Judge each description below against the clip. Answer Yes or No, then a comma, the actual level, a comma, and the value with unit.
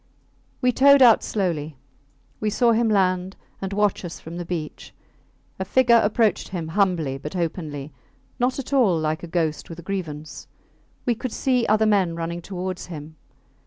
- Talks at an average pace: Yes, average, 165 wpm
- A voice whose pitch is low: No, medium, 185 Hz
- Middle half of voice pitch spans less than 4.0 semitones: No, average, 5.1 semitones